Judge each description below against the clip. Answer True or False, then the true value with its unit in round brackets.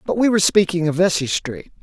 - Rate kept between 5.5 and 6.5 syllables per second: True (6.1 syllables/s)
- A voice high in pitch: False (175 Hz)